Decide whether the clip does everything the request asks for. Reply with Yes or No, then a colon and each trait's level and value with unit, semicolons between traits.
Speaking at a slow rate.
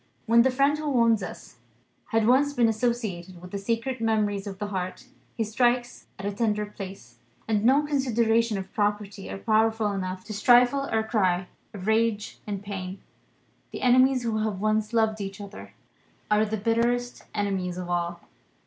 No: average, 170 wpm